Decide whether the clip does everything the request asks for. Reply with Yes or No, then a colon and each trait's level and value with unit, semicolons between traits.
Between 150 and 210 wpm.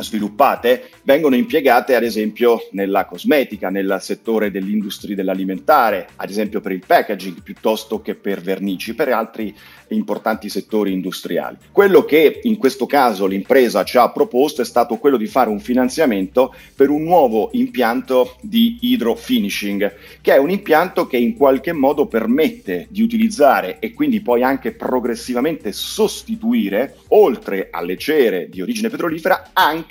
No: average, 140 wpm